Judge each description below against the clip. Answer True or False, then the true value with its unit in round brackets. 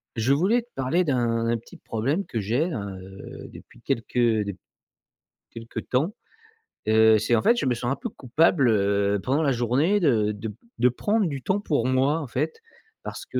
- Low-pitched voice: True (125 Hz)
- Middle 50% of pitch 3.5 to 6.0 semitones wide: True (5.6 semitones)